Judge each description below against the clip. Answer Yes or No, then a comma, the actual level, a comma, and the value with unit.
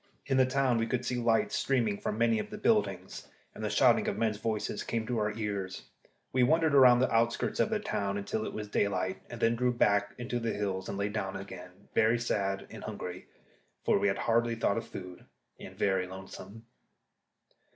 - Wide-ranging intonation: No, average, 3.1 semitones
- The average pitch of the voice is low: Yes, low, 110 Hz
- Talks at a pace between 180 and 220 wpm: Yes, fast, 205 wpm